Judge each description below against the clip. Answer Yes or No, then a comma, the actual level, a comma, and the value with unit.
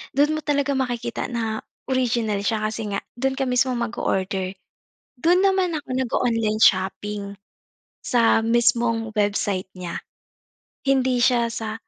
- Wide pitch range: No, average, 3.5 semitones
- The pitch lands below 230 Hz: No, high, 235 Hz